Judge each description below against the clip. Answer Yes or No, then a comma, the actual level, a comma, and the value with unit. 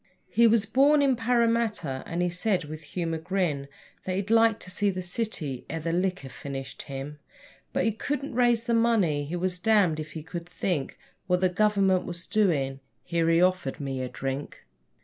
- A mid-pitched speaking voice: Yes, medium, 180 Hz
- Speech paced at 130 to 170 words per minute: No, average, 190 wpm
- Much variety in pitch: Yes, wide, 6.0 semitones